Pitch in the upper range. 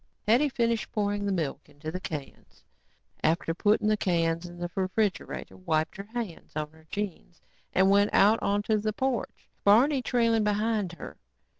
Yes: high, 200 Hz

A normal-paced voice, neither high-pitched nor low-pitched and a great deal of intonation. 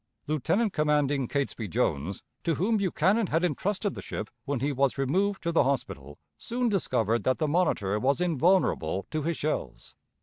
Yes: average, 165 wpm; medium, 150 Hz; wide, 5.8 semitones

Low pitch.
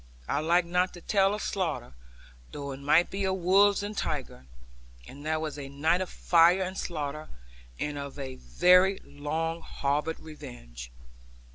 No: medium, 160 Hz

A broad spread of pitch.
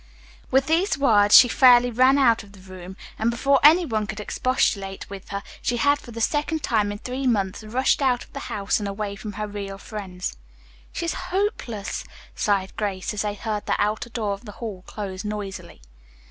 No: average, 4.2 semitones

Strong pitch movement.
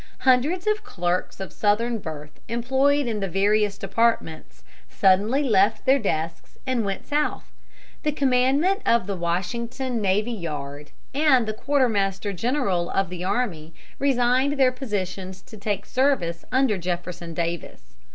Yes: wide, 6.2 semitones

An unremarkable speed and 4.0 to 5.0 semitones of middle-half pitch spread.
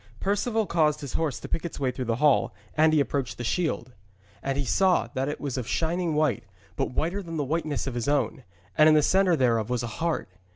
No: fast, 235 wpm; average, 4.5 semitones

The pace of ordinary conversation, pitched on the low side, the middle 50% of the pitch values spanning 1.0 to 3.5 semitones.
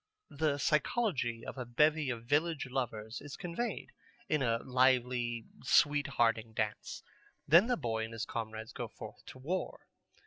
No: average, 150 wpm; low, 130 Hz; average, 4.7 semitones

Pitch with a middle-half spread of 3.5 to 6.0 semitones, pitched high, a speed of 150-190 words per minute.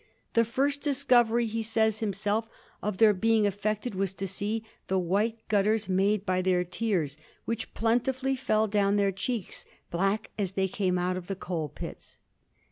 No: average, 2.9 semitones; high, 210 Hz; average, 165 wpm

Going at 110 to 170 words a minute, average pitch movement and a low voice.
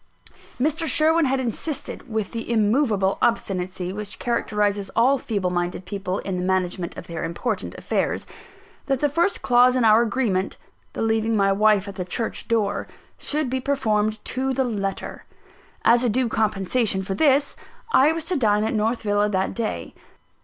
No: average, 165 wpm; average, 4.6 semitones; high, 220 Hz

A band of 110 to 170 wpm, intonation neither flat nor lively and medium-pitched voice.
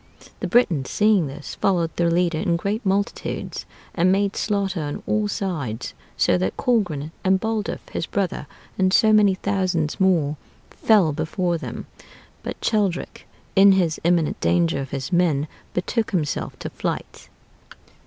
Yes: average, 145 wpm; average, 4.3 semitones; medium, 180 Hz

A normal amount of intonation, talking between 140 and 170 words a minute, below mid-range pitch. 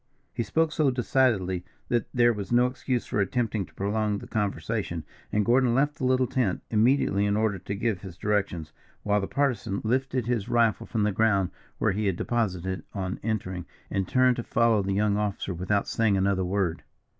No: average, 3.6 semitones; average, 190 wpm; low, 105 Hz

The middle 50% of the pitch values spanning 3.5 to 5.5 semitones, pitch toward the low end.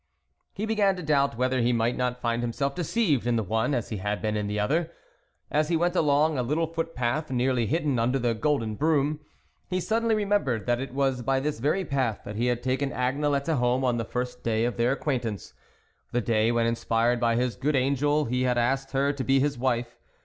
Yes: average, 3.8 semitones; low, 130 Hz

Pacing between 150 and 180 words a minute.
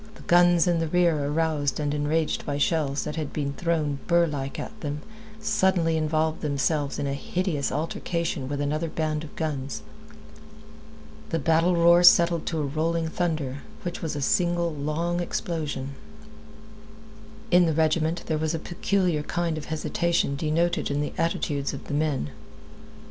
Yes: average, 160 wpm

